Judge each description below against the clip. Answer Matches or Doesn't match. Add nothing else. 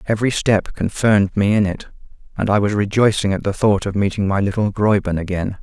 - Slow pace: Doesn't match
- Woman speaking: Doesn't match